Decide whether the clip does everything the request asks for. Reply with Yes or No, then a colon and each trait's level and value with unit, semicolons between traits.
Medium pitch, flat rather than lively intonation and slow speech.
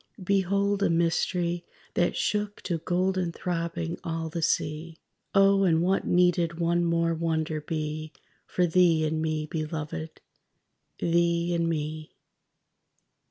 Yes: medium, 170 Hz; narrow, 1.9 semitones; slow, 125 wpm